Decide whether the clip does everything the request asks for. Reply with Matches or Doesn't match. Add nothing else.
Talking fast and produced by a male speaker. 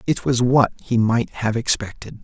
Doesn't match